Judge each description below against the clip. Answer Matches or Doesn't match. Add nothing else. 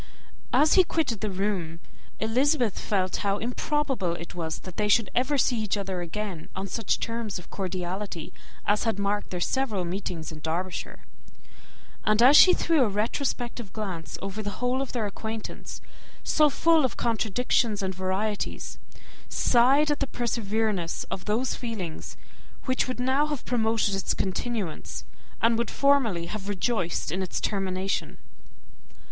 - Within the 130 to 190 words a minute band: Matches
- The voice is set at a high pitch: Matches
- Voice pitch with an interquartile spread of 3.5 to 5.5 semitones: Matches